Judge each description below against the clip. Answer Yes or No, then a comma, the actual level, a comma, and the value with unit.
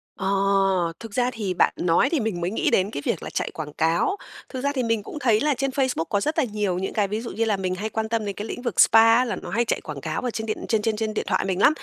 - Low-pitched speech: No, high, 220 Hz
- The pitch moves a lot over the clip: No, average, 3.9 semitones